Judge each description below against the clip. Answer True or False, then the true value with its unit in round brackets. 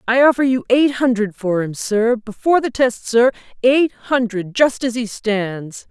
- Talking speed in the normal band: True (185 wpm)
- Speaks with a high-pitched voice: True (235 Hz)